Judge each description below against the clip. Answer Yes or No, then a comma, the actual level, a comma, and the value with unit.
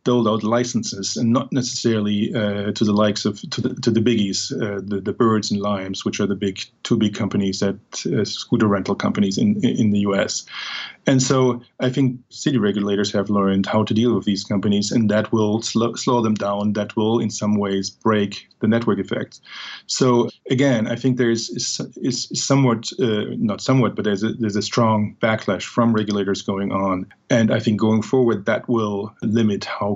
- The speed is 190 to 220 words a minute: Yes, average, 200 wpm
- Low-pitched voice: Yes, low, 110 Hz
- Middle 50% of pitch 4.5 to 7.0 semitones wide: No, average, 2.8 semitones